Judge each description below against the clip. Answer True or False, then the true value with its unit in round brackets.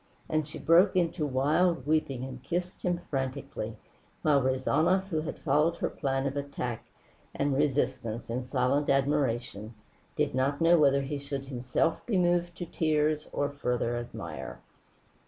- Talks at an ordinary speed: True (150 wpm)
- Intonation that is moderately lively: True (3.6 semitones)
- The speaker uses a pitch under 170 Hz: True (140 Hz)